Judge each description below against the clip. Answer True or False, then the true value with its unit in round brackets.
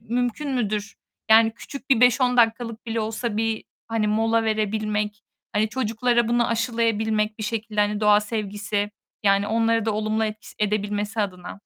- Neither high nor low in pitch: False (220 Hz)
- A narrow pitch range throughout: True (1.5 semitones)